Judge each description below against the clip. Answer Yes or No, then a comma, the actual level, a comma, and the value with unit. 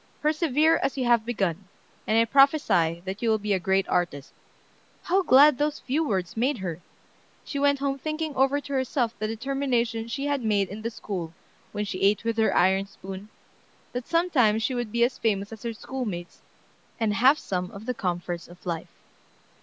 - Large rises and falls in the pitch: Yes, wide, 5.9 semitones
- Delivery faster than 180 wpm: Yes, average, 190 wpm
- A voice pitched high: Yes, high, 230 Hz